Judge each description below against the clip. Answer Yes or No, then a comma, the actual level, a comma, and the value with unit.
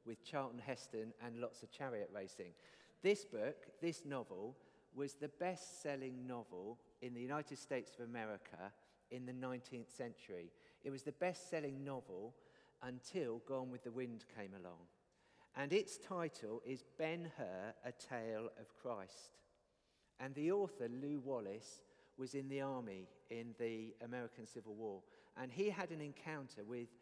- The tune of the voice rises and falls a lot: No, average, 4.1 semitones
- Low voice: Yes, low, 130 Hz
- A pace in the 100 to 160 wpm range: Yes, average, 155 wpm